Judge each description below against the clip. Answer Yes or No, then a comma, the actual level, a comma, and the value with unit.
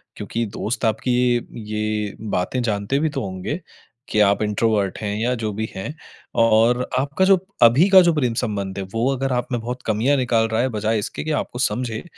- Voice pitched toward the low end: Yes, low, 115 Hz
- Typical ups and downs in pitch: Yes, average, 3.0 semitones